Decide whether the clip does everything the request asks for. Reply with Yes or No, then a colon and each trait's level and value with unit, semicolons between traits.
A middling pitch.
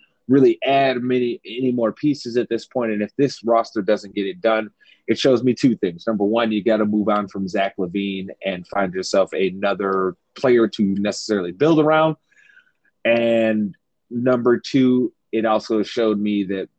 No: low, 110 Hz